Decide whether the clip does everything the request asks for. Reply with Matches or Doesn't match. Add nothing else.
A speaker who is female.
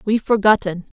Matches